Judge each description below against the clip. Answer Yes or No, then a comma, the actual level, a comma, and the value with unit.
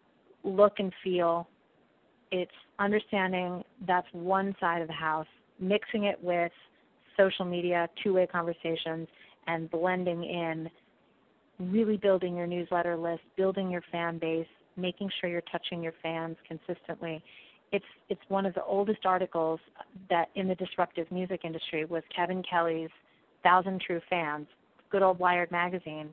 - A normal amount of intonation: No, narrow, 2.1 semitones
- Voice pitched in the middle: Yes, medium, 175 Hz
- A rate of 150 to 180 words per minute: No, average, 140 wpm